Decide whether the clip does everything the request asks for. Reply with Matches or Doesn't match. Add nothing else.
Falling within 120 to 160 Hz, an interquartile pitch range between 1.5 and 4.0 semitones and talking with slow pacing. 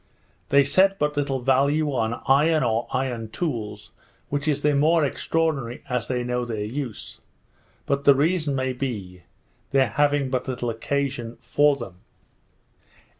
Doesn't match